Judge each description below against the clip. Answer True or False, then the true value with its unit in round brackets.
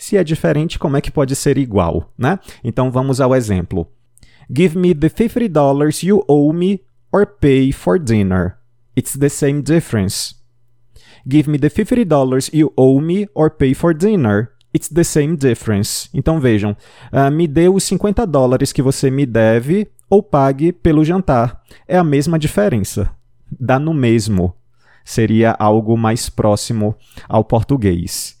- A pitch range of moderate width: False (5.7 semitones)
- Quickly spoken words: False (155 wpm)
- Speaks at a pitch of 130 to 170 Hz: True (135 Hz)